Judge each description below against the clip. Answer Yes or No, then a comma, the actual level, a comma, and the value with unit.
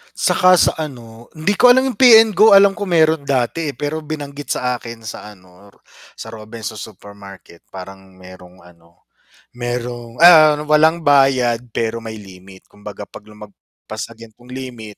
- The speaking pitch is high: No, low, 120 Hz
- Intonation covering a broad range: Yes, wide, 6.8 semitones